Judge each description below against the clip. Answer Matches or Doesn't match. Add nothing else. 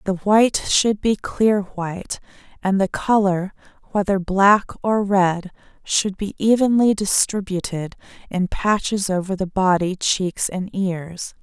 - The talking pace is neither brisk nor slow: Doesn't match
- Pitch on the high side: Matches